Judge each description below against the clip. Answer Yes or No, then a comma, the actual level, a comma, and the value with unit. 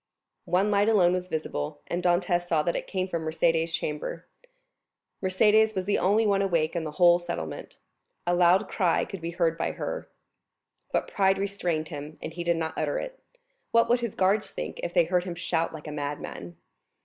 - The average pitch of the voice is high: No, medium, 175 Hz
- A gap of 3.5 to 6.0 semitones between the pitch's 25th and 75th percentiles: No, average, 3.0 semitones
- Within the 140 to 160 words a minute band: No, average, 195 wpm